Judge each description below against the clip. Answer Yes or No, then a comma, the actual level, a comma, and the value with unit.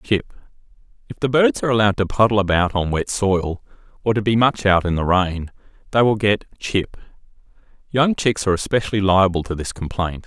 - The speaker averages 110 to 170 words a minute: No, average, 180 wpm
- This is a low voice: Yes, low, 100 Hz